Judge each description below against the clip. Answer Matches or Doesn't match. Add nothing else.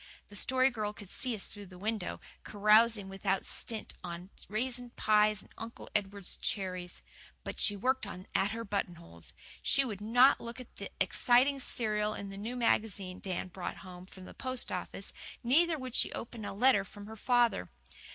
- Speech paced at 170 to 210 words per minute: Matches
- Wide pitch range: Doesn't match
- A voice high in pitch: Matches